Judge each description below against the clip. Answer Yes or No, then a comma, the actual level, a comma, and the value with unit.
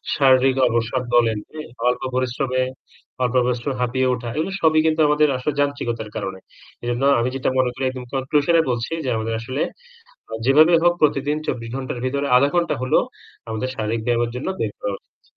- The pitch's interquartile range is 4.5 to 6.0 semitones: No, average, 3.1 semitones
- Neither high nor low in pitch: No, low, 130 Hz